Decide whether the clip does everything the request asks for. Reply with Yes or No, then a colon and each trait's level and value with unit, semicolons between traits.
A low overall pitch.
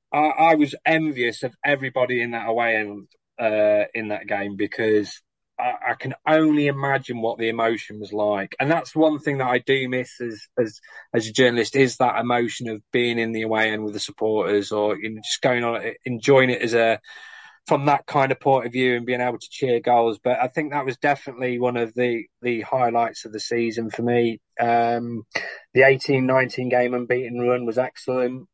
Yes: low, 120 Hz